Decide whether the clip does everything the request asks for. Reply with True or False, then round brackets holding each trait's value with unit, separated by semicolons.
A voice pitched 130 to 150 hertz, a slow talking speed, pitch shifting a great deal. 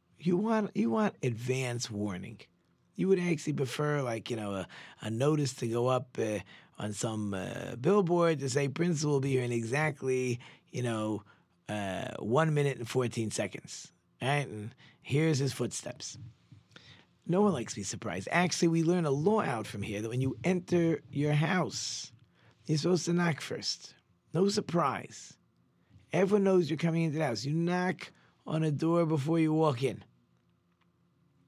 False (140 Hz; 170 wpm; 6.1 semitones)